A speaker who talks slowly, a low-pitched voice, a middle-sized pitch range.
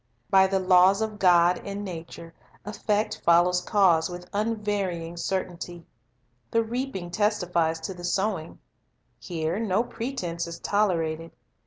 No: slow, 125 wpm; medium, 185 Hz; average, 3.4 semitones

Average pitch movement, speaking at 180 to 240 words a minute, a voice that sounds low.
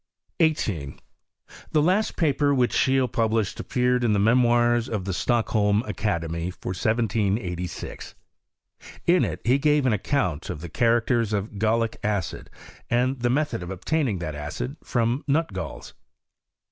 No: average, 4.7 semitones; average, 145 wpm; low, 115 Hz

